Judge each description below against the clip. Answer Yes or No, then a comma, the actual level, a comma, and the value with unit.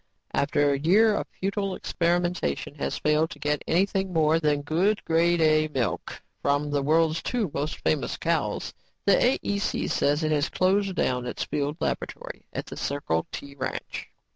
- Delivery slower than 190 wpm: Yes, average, 165 wpm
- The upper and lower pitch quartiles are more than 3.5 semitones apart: Yes, average, 4.2 semitones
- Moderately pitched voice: Yes, medium, 155 Hz